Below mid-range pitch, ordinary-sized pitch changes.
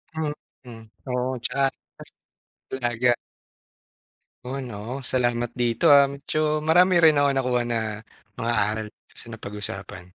Yes: low, 125 Hz; average, 3.3 semitones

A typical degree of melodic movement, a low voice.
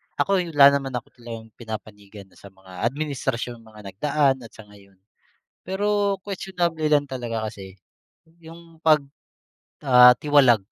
No: wide, 6.1 semitones; low, 130 Hz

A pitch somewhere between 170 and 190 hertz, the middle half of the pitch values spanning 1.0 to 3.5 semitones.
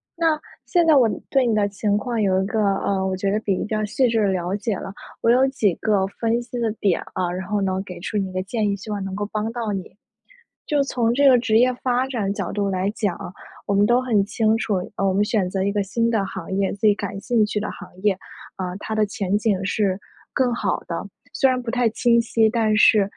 No: high, 210 Hz; average, 3.0 semitones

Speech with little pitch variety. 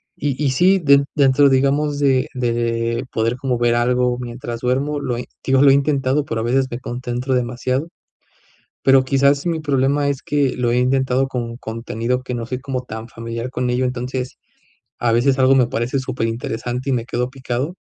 Yes: narrow, 2.1 semitones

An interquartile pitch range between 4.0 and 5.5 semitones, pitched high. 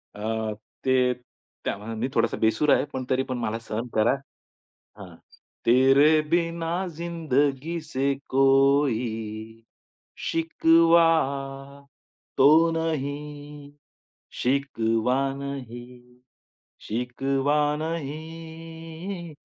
No: average, 4.8 semitones; medium, 140 Hz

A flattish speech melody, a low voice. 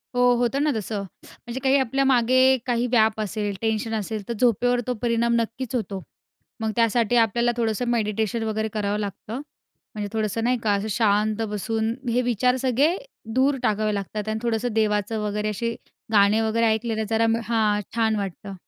No: narrow, 2.2 semitones; high, 225 Hz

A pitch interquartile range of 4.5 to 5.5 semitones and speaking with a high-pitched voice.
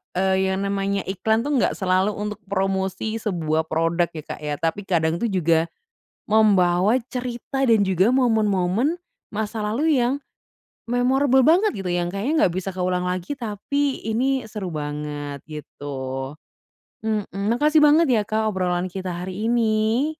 Yes: average, 4.8 semitones; high, 200 Hz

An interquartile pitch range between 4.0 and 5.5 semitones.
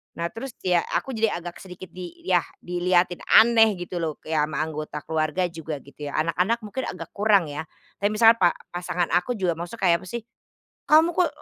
Yes: average, 4.5 semitones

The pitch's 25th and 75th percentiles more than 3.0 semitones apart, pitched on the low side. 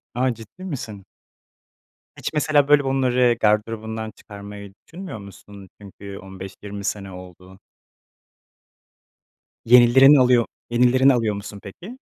Yes: average, 4.5 semitones; low, 110 Hz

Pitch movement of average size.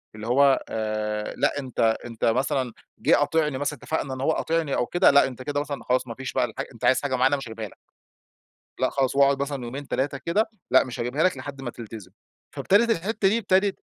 Yes: average, 3.3 semitones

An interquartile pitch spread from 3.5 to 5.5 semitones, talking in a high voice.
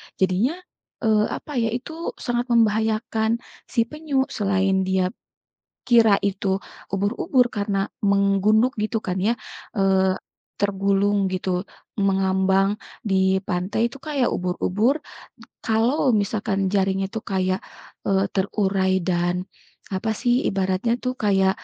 No: average, 3.0 semitones; high, 200 Hz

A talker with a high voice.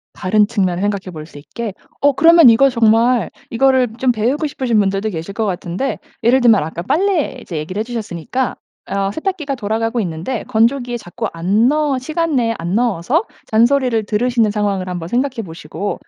Yes: high, 225 Hz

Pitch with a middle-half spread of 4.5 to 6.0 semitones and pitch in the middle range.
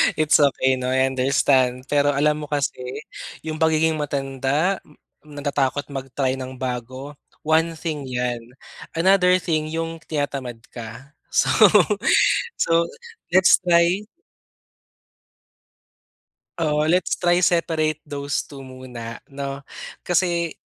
No: average, 3.5 semitones; medium, 145 Hz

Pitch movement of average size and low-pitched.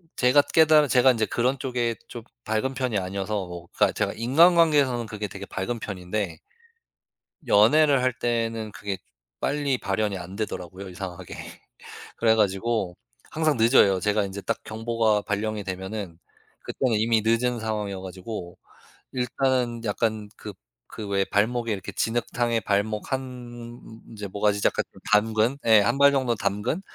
Yes: average, 3.5 semitones; low, 110 Hz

